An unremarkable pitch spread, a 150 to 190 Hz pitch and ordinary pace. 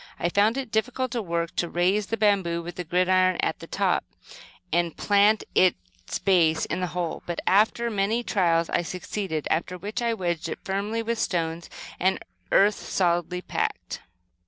Yes: average, 3.6 semitones; medium, 185 Hz; average, 165 wpm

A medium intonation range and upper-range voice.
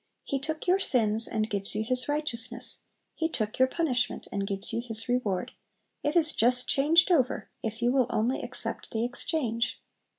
Yes: average, 4.6 semitones; high, 245 Hz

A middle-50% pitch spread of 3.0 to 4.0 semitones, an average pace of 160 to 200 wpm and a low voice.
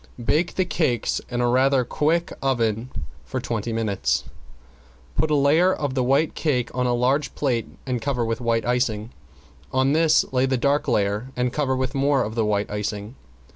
Yes: average, 3.5 semitones; average, 180 wpm; low, 125 Hz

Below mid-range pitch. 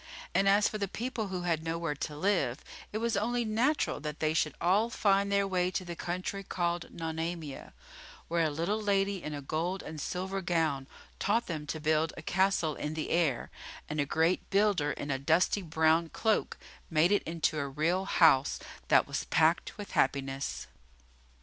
No: medium, 170 Hz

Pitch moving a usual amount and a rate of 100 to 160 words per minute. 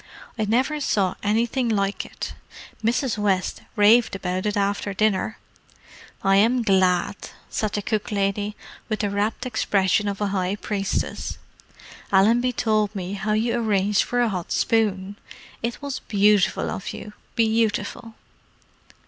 No: narrow, 2.3 semitones; average, 140 wpm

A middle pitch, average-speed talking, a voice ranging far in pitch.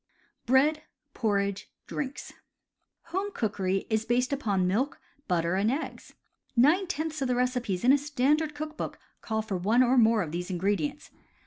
No: high, 240 Hz; average, 155 wpm; wide, 6.3 semitones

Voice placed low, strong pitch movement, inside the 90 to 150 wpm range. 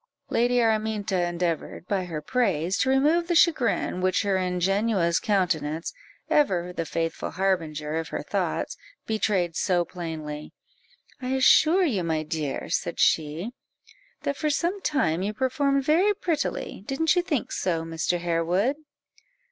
No: high, 190 Hz; wide, 7.9 semitones; average, 140 wpm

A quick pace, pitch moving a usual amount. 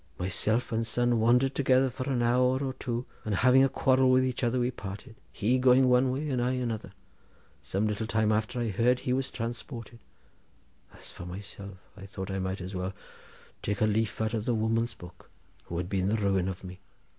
Yes: fast, 210 wpm; average, 4.0 semitones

